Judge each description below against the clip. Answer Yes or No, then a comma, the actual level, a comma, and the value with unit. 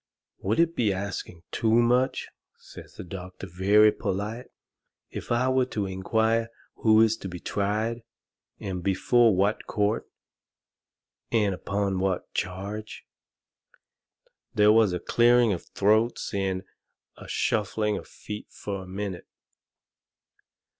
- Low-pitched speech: Yes, low, 105 Hz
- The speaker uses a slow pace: Yes, slow, 125 wpm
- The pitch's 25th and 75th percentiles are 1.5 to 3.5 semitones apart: Yes, average, 2.8 semitones